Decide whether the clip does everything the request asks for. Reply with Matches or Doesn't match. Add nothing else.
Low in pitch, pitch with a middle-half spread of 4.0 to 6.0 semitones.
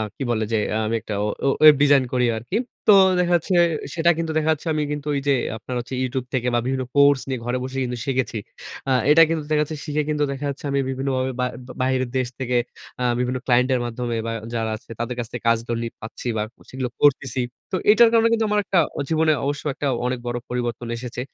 Doesn't match